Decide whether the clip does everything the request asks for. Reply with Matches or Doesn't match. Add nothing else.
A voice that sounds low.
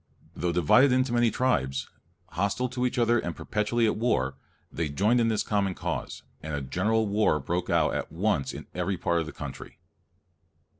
Matches